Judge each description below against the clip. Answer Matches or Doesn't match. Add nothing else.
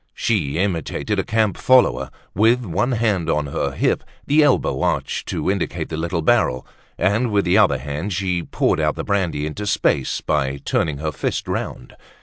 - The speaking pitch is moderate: Doesn't match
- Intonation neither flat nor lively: Doesn't match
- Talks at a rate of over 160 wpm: Matches